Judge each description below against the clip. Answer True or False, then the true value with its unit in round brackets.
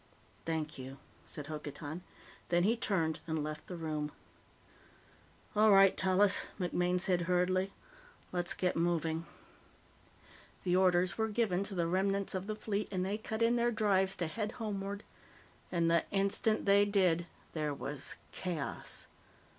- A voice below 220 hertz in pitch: True (185 Hz)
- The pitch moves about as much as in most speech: True (3.3 semitones)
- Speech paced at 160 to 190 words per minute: False (145 wpm)